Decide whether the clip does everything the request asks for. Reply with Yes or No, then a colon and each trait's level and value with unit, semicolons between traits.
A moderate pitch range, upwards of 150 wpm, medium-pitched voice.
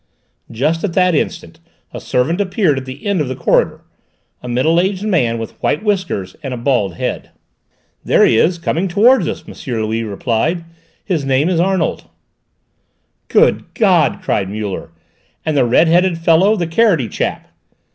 No: wide, 6.8 semitones; average, 165 wpm; medium, 160 Hz